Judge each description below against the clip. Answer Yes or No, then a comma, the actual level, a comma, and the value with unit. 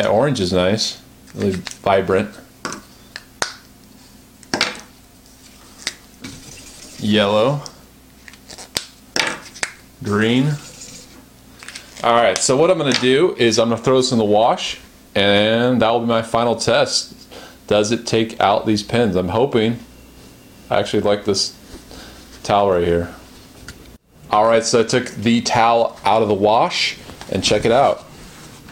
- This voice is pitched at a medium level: No, low, 115 Hz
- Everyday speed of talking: No, slow, 125 wpm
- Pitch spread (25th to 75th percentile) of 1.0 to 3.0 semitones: Yes, narrow, 2.4 semitones